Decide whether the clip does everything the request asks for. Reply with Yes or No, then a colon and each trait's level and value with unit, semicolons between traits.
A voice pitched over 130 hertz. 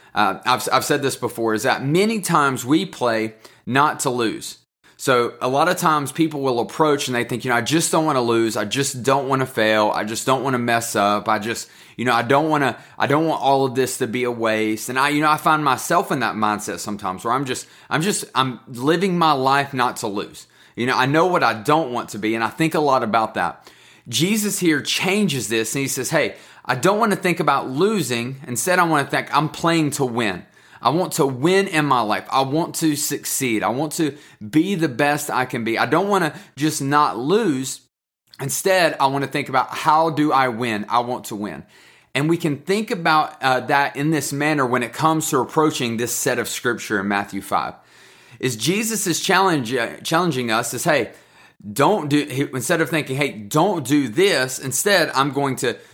Yes: medium, 140 Hz